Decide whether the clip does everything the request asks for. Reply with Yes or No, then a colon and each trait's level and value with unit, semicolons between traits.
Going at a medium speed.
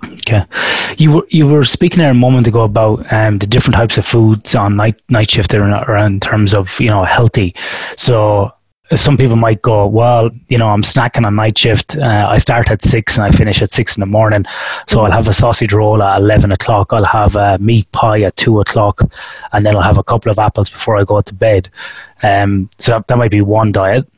No: fast, 230 wpm